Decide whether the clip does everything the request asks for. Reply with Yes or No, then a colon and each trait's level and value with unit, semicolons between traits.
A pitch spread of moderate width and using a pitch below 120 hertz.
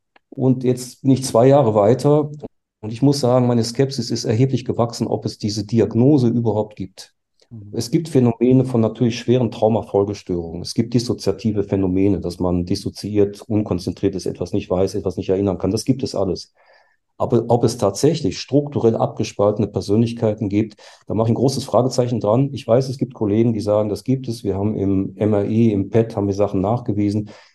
Yes: average, 3.6 semitones; low, 110 Hz